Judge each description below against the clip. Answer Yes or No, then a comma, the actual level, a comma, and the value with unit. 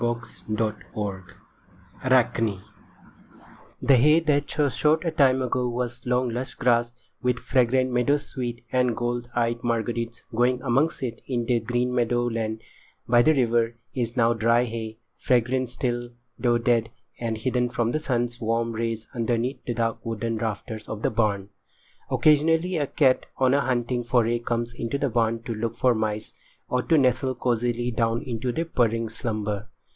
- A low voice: Yes, low, 120 Hz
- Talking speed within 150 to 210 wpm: Yes, average, 160 wpm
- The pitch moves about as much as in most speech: No, narrow, 1.8 semitones